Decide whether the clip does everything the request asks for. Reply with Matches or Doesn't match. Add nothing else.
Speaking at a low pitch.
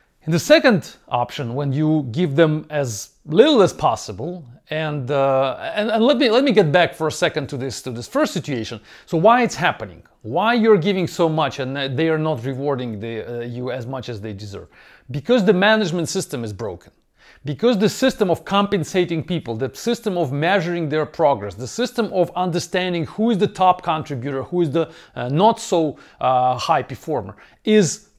Doesn't match